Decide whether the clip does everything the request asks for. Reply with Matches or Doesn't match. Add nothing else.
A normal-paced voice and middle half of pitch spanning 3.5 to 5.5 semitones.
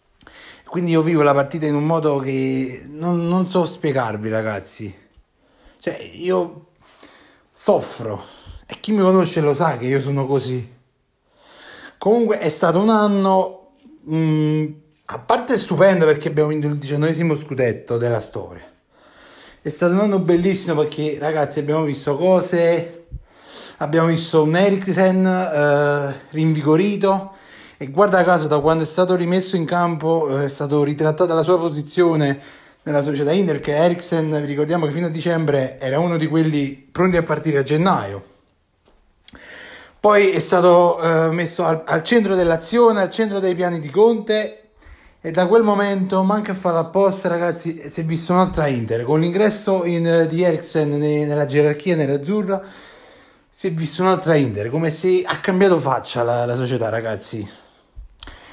Matches